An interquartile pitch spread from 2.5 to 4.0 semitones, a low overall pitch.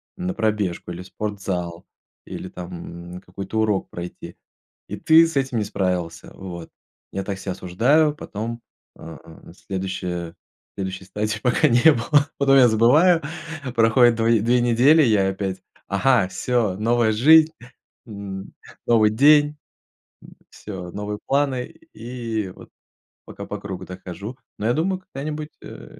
No: wide, 5.5 semitones; low, 110 Hz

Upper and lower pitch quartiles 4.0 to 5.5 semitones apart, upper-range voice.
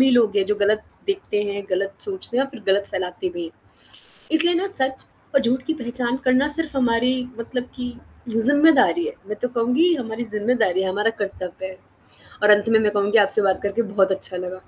Yes: average, 4.6 semitones; high, 225 Hz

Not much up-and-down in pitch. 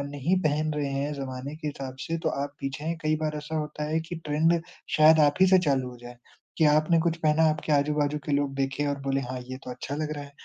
Yes: narrow, 2.0 semitones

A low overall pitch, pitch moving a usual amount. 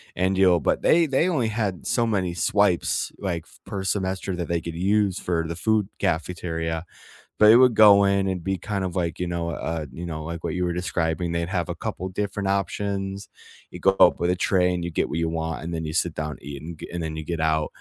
Yes: very low, 90 Hz; average, 3.0 semitones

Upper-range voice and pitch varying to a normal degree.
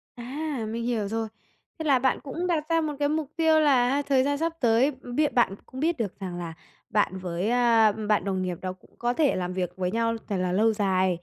No: high, 230 Hz; wide, 7.0 semitones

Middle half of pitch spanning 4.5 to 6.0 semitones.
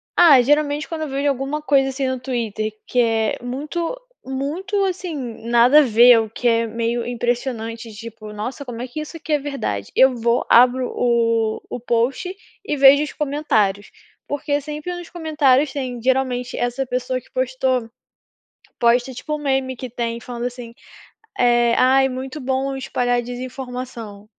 No: average, 3.0 semitones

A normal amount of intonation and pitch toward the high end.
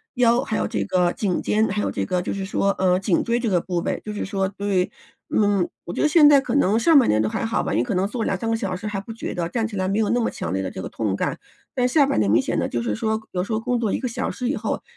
Yes: average, 4.3 semitones; high, 205 Hz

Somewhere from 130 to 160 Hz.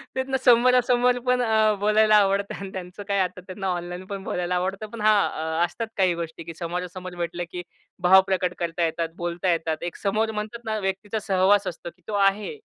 No: high, 190 Hz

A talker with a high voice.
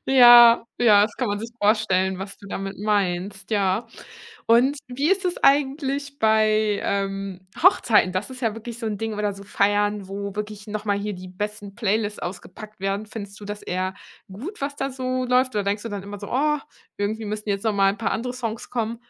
Yes: high, 210 Hz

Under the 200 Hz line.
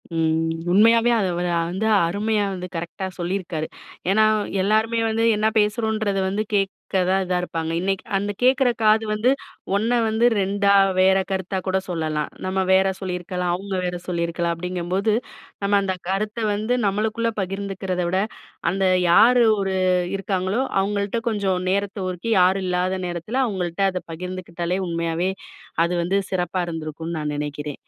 Yes: high, 190 Hz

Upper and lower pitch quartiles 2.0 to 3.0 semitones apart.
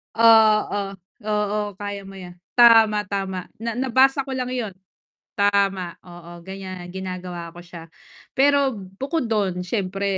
No: average, 3.7 semitones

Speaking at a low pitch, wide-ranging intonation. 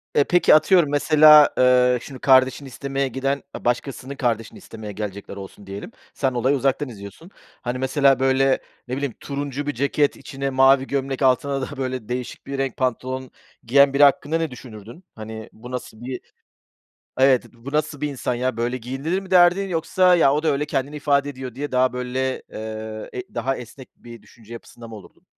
No: low, 130 Hz; narrow, 2.5 semitones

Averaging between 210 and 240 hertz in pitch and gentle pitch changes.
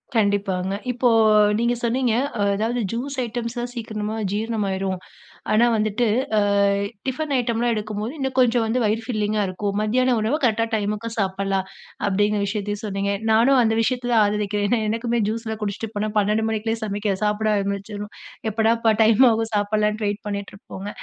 Yes: high, 215 Hz; narrow, 2.2 semitones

